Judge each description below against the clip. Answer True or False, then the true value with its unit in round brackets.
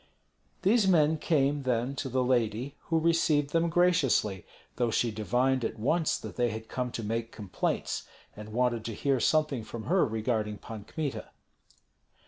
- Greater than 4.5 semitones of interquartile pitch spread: True (5.2 semitones)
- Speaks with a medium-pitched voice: False (125 Hz)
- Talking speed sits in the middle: True (160 wpm)